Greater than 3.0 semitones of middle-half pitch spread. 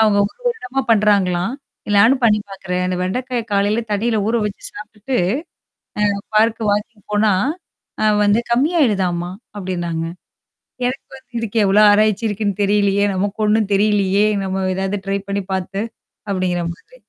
No: narrow, 2.5 semitones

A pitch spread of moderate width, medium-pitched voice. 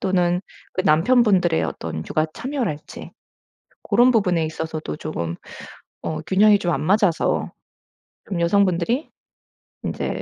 Yes: average, 4.5 semitones; medium, 180 Hz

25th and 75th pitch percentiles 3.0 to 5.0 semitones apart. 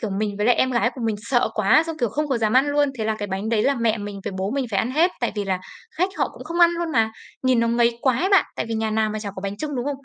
Yes: average, 4.6 semitones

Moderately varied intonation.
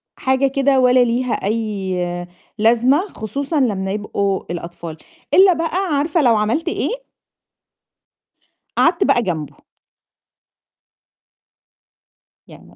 No: wide, 6.3 semitones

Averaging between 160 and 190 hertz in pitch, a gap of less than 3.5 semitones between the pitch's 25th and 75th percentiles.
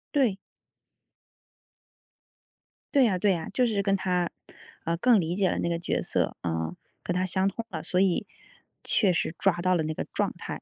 Yes: medium, 185 Hz; average, 2.8 semitones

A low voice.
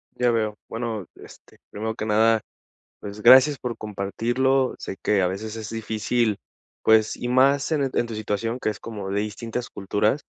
Yes: low, 110 Hz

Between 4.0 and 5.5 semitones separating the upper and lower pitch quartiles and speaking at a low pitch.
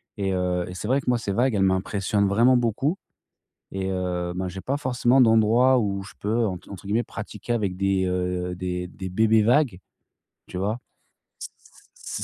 Yes: average, 4.3 semitones; low, 100 Hz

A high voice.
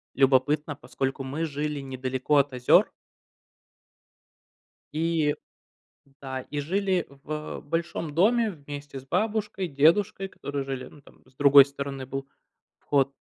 No: medium, 145 Hz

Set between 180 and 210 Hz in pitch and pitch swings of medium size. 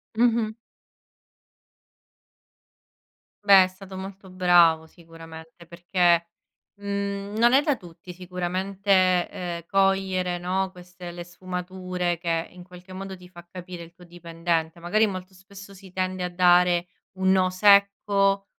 No: medium, 185 Hz; narrow, 1.9 semitones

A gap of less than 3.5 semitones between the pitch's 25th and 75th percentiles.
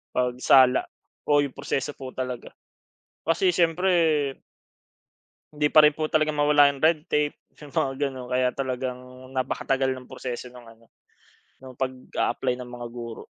Yes: average, 2.9 semitones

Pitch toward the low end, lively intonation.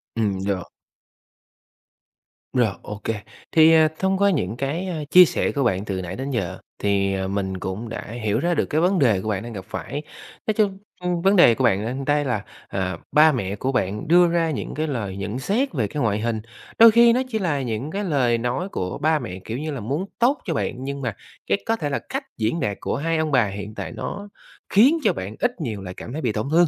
Yes: low, 130 Hz; wide, 8.3 semitones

